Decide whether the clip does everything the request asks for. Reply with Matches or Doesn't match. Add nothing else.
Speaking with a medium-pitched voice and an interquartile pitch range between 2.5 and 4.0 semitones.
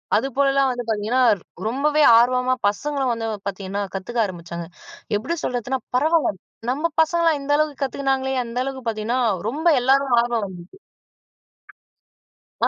Doesn't match